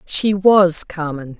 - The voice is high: No, medium, 175 Hz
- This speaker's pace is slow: Yes, slow, 130 wpm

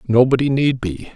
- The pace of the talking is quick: No, average, 155 wpm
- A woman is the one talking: No, male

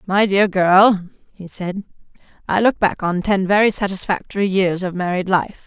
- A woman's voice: Yes, female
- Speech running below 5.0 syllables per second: Yes, 4.8 syllables/s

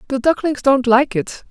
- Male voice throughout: No, female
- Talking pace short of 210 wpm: Yes, average, 200 wpm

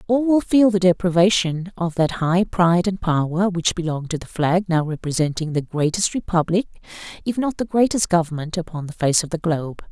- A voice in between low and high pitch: Yes, medium, 175 Hz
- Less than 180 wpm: No, average, 195 wpm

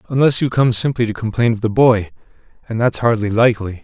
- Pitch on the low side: Yes, low, 115 Hz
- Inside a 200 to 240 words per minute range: Yes, fast, 205 wpm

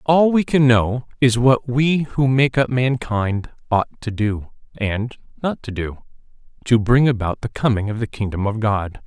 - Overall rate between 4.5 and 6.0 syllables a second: No, 4.3 syllables/s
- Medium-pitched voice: No, low, 120 Hz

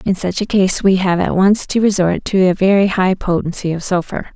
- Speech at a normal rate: No, fast, 235 wpm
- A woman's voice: Yes, female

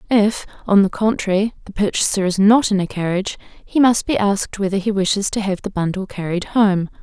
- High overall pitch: Yes, high, 200 Hz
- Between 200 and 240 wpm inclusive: Yes, fast, 205 wpm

